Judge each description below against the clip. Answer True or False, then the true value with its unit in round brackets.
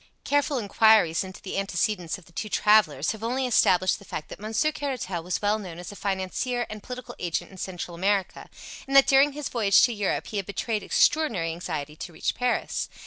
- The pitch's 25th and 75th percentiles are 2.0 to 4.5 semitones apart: False (5.1 semitones)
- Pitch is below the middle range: False (205 Hz)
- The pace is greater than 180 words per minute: True (200 wpm)